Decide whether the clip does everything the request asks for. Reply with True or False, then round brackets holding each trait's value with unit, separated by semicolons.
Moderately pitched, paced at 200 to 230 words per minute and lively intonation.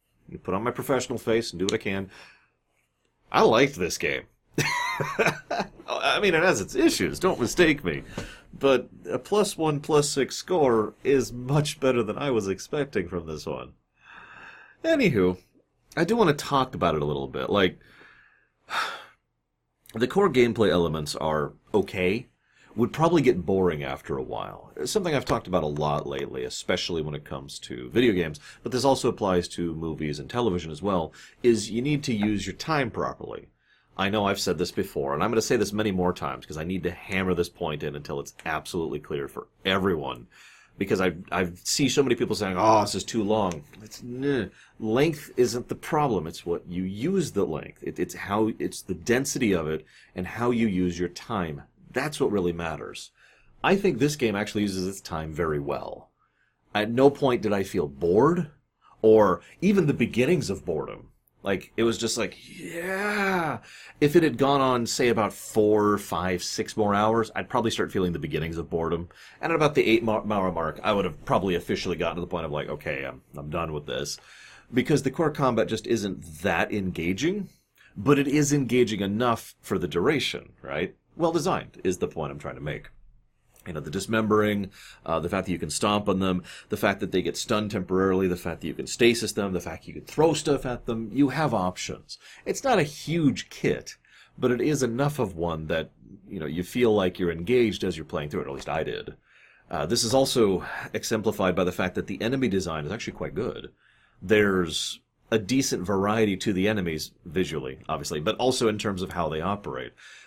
False (105 Hz; 205 wpm; 6.0 semitones)